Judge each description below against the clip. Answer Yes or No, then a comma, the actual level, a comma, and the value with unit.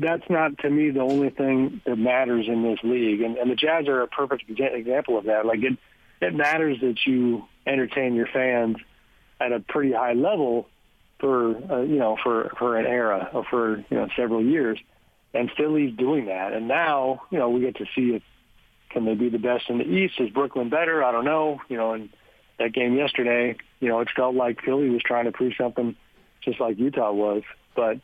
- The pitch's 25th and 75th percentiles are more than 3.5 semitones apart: No, narrow, 2.5 semitones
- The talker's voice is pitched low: Yes, low, 125 Hz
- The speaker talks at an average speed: No, fast, 210 wpm